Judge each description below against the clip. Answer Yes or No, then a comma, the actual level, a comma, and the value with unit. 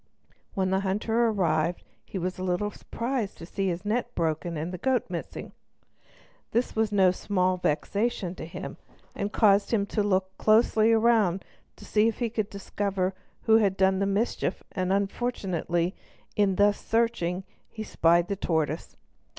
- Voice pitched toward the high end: Yes, high, 195 Hz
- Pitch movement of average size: Yes, average, 3.1 semitones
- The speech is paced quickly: No, average, 160 wpm